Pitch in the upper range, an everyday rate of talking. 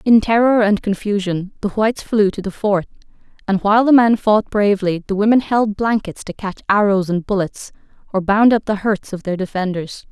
Yes: high, 205 Hz; average, 195 wpm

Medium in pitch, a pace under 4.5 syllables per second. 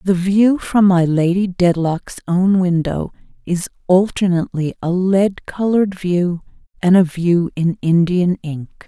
Yes: medium, 180 Hz; 4.0 syllables/s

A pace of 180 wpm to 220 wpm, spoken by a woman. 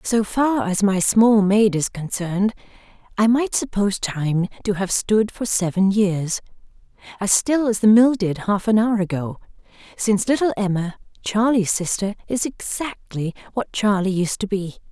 No: average, 160 wpm; female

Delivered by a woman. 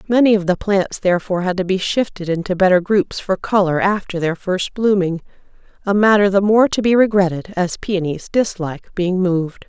Yes: female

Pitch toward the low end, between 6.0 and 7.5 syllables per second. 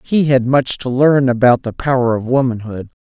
No: low, 130 Hz; 5.0 syllables/s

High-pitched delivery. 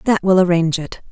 No: medium, 180 Hz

